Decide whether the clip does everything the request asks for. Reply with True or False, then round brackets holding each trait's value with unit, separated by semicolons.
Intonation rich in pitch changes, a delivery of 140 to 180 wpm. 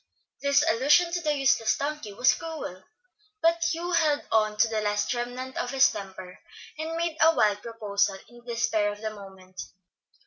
True (6.5 semitones; 175 wpm)